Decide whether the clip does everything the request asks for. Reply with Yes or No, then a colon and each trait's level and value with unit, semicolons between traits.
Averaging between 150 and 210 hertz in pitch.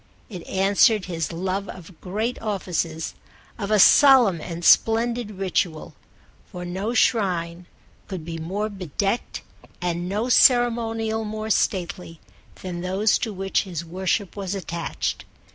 Yes: high, 190 Hz